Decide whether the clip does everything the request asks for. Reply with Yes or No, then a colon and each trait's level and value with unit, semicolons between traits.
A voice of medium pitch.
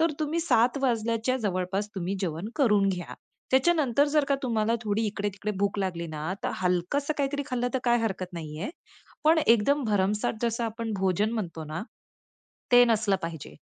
No: high, 215 Hz